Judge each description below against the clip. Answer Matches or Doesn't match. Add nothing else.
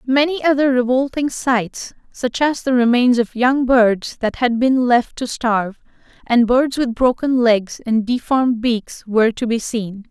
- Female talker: Matches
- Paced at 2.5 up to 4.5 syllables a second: Matches